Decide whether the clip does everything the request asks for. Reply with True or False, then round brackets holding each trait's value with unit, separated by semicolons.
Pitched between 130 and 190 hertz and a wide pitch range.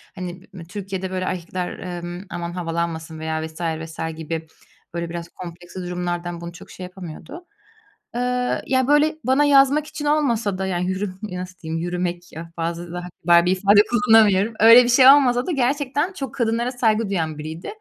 True (185 Hz; 5.9 semitones)